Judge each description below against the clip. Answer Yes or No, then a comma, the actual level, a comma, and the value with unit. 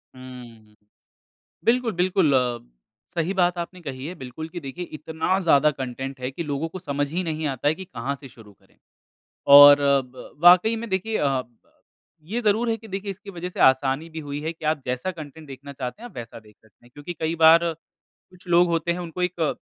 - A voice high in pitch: No, medium, 160 Hz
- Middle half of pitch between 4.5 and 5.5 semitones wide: Yes, average, 5.0 semitones